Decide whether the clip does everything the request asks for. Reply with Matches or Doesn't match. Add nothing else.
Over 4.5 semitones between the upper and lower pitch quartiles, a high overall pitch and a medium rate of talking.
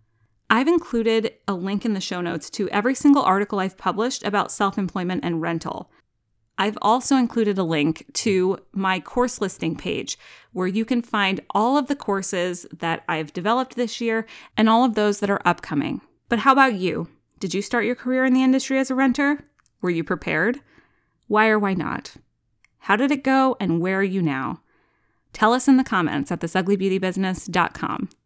Matches